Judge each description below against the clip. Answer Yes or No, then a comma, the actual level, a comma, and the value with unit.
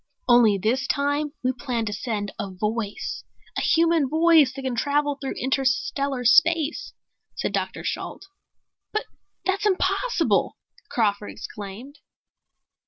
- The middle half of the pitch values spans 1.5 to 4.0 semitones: No, average, 5.0 semitones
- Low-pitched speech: No, very high, 265 Hz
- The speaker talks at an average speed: No, slow, 120 wpm